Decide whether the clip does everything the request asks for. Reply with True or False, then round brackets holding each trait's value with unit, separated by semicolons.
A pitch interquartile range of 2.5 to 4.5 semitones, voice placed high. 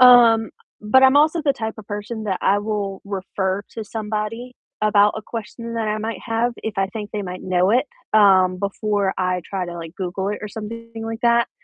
True (2.8 semitones; 210 Hz)